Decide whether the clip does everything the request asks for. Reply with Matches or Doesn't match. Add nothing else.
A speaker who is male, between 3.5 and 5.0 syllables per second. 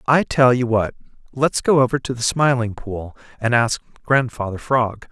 Matches